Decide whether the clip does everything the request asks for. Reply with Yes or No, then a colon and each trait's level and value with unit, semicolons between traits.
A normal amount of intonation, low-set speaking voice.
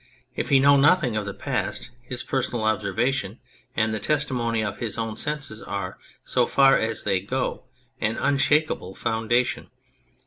Yes: average, 4.0 semitones; low, 120 Hz